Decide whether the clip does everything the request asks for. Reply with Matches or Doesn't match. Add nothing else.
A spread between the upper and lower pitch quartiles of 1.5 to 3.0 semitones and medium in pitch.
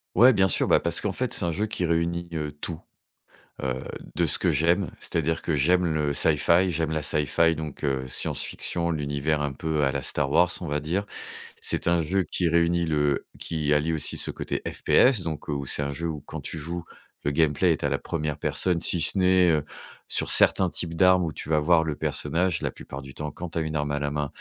Doesn't match